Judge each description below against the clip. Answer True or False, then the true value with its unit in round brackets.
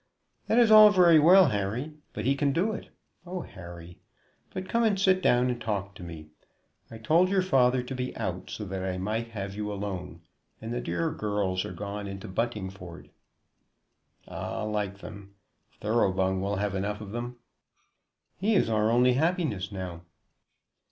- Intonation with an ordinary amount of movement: False (6.8 semitones)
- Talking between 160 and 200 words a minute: True (170 wpm)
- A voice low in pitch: True (110 Hz)